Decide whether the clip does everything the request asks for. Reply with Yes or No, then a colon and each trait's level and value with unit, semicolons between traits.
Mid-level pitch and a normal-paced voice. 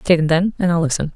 No: medium, 170 Hz; fast, 310 wpm